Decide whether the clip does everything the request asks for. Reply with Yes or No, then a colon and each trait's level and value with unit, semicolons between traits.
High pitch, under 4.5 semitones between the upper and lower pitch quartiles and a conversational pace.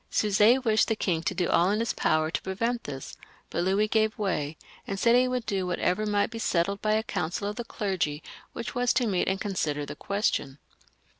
No: high, 200 Hz; average, 3.9 semitones; fast, 215 wpm